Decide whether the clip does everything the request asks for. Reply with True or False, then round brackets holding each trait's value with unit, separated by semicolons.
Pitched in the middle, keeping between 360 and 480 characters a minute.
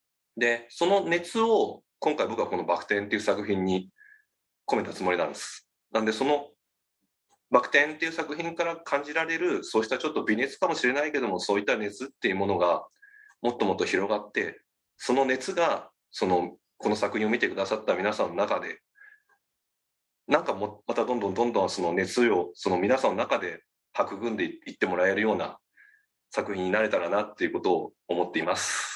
True (170 Hz; 375 characters per minute)